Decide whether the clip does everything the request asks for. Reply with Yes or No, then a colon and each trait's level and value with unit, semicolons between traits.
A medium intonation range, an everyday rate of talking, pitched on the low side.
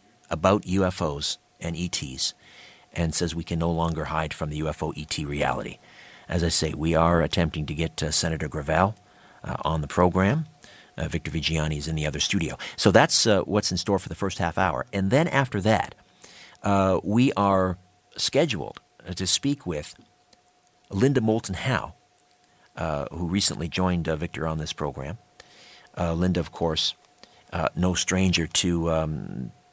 Yes: average, 3.4 semitones; average, 165 wpm; very low, 85 Hz